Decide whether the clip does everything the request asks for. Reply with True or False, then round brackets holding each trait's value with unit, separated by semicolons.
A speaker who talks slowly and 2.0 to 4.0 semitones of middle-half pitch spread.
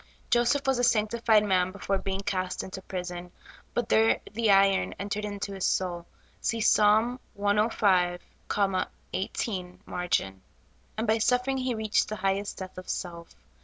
False (145 wpm; 3.2 semitones)